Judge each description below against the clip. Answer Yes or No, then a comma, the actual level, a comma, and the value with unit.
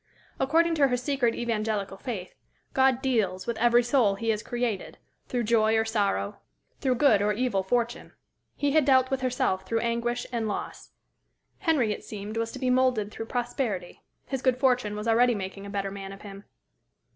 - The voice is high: Yes, high, 235 Hz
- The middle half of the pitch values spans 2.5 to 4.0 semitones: Yes, average, 3.6 semitones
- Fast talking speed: No, average, 180 wpm